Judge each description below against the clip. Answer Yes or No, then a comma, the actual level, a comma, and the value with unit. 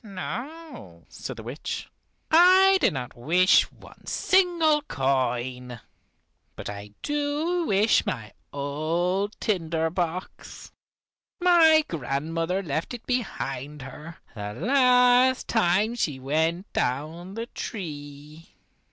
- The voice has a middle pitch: Yes, medium, 175 Hz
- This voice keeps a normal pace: No, slow, 105 wpm